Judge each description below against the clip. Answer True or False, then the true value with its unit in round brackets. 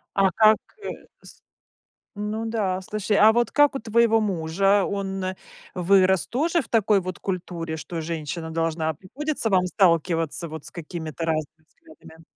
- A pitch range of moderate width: True (4.5 semitones)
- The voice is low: False (185 Hz)